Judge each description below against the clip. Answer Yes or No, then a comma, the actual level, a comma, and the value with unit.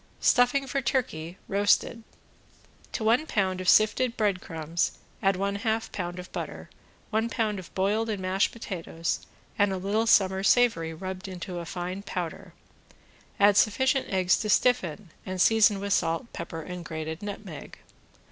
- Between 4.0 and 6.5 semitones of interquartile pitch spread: No, average, 3.5 semitones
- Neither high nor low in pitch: No, high, 195 Hz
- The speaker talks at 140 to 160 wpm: Yes, average, 150 wpm